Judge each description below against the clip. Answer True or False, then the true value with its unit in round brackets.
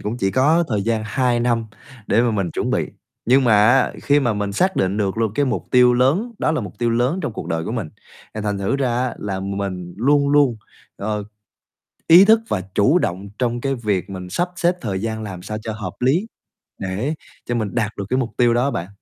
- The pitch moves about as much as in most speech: True (4.6 semitones)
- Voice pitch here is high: False (115 Hz)